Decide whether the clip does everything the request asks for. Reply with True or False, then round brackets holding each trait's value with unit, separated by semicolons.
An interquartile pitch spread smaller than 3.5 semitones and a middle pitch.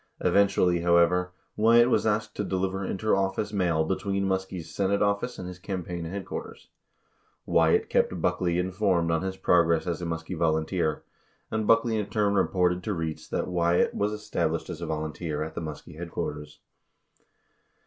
False (3.1 semitones; 90 Hz)